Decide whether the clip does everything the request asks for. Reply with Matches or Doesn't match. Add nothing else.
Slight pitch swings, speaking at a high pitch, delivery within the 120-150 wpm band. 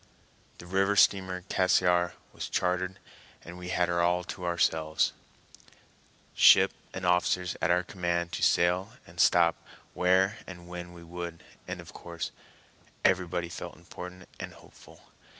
Doesn't match